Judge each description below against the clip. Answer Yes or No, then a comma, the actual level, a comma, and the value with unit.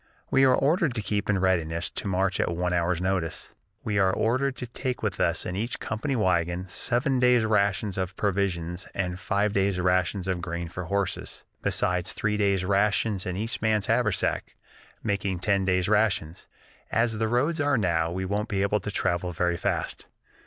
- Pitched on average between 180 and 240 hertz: No, low, 100 Hz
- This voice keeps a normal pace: Yes, average, 185 wpm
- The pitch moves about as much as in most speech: Yes, average, 3.3 semitones